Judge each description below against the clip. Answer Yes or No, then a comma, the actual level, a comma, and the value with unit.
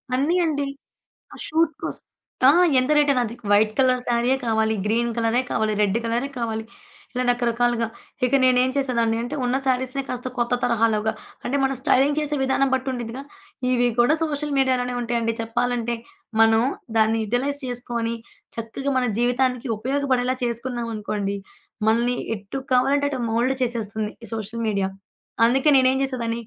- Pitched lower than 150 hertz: No, high, 245 Hz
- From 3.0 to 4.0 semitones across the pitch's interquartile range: No, narrow, 2.5 semitones